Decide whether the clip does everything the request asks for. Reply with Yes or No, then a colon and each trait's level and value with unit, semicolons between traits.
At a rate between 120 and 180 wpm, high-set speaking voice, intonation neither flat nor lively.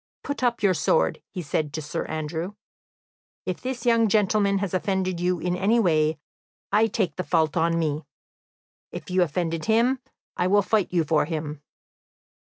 No: average, 165 wpm; medium, 180 Hz; average, 4.7 semitones